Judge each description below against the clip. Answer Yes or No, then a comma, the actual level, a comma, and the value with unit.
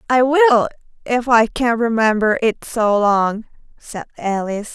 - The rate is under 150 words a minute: Yes, average, 140 wpm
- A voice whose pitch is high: Yes, high, 230 Hz